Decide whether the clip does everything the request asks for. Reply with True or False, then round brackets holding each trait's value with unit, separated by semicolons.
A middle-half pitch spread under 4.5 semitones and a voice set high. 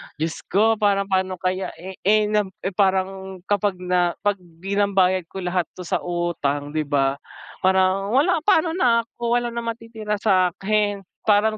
True (2.7 semitones; 195 Hz)